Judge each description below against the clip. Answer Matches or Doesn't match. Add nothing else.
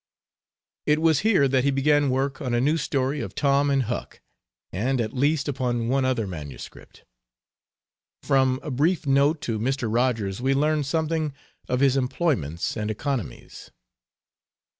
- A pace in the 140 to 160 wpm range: Matches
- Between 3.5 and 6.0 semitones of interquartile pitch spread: Doesn't match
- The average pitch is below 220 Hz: Matches